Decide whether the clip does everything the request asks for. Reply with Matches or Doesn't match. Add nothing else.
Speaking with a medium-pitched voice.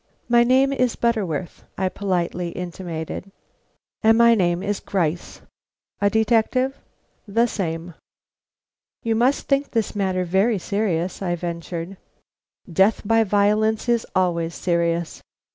Doesn't match